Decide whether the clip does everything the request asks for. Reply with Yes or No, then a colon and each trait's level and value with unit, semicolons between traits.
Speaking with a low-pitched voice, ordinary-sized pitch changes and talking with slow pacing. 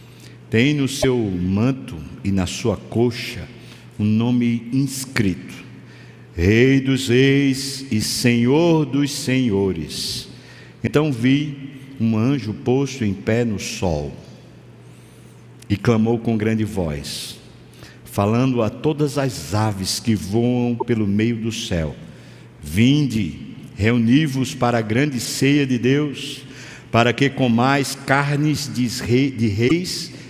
Yes: low, 120 Hz; average, 4.1 semitones; slow, 115 wpm